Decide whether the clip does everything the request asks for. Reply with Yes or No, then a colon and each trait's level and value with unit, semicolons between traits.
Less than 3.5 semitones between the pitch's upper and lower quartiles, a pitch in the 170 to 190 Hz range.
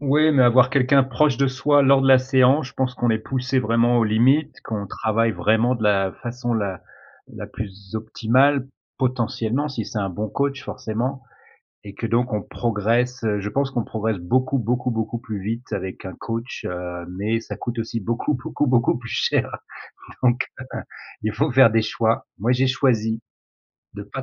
No: average, 3.1 semitones; low, 120 Hz